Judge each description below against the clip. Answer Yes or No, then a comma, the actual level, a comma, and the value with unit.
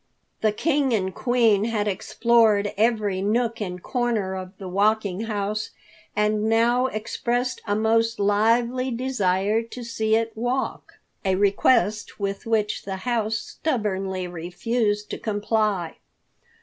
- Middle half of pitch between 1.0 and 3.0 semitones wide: Yes, narrow, 2.5 semitones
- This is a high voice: Yes, high, 215 Hz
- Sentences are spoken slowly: Yes, slow, 125 wpm